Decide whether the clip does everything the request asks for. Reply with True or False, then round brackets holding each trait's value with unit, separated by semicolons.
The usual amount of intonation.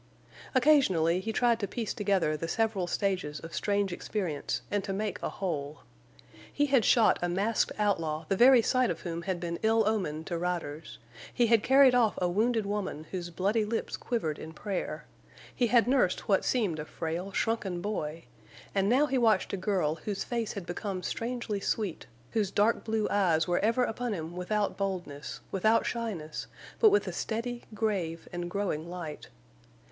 True (4.5 semitones)